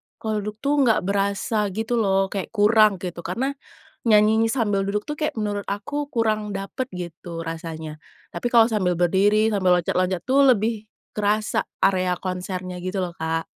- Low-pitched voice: No, high, 205 Hz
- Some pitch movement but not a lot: Yes, average, 3.2 semitones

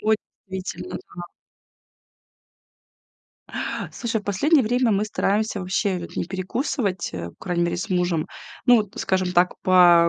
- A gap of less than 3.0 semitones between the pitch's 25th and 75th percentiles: No, average, 3.6 semitones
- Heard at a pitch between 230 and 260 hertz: No, high, 190 Hz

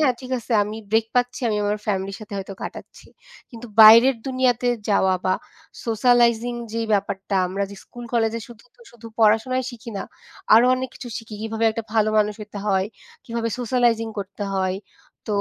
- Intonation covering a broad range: No, average, 2.7 semitones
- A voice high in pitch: Yes, high, 225 Hz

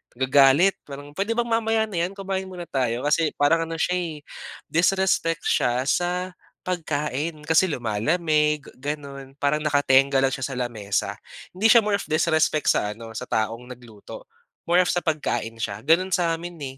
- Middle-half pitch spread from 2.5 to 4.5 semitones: No, average, 5.0 semitones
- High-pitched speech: No, medium, 150 Hz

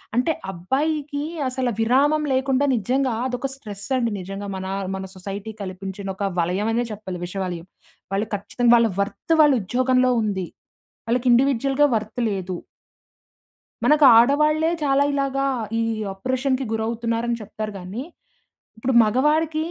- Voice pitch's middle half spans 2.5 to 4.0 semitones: No, average, 5.3 semitones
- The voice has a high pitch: Yes, high, 235 Hz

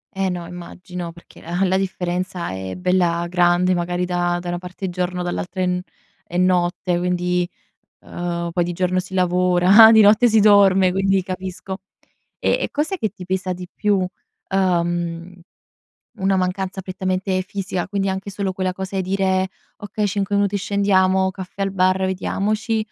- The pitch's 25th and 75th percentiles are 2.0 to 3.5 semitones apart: No, narrow, 1.4 semitones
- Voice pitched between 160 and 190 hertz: Yes, medium, 185 Hz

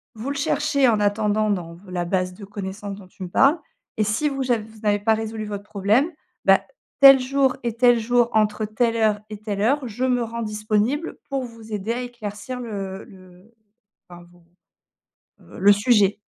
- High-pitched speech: Yes, high, 215 Hz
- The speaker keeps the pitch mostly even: No, average, 3.2 semitones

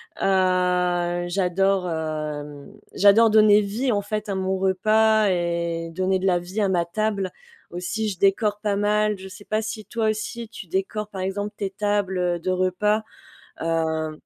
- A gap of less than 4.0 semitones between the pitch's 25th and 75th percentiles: Yes, average, 2.9 semitones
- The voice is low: No, high, 190 Hz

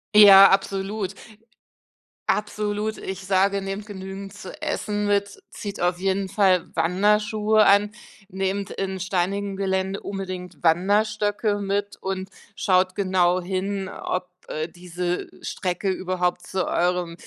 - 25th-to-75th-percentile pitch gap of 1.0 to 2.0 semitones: Yes, narrow, 1.7 semitones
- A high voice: Yes, high, 195 Hz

